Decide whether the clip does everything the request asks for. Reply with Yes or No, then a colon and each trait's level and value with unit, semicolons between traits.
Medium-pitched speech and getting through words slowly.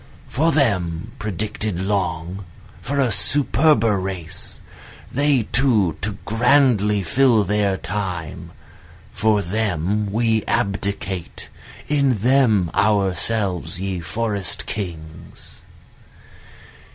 No: low, 105 Hz; slow, 90 wpm